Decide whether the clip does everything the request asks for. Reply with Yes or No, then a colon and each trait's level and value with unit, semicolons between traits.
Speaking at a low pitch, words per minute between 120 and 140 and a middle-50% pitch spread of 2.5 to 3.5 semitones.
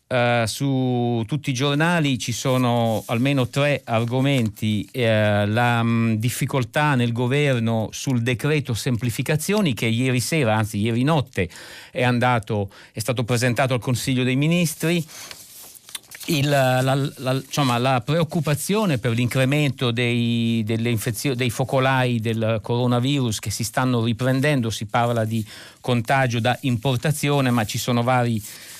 Yes: low, 125 Hz; average, 130 wpm; average, 2.9 semitones